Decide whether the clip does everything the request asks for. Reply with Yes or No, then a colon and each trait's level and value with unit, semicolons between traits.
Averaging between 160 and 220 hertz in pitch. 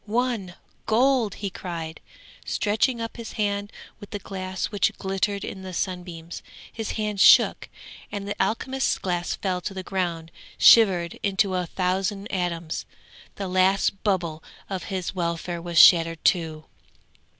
Yes: high, 190 Hz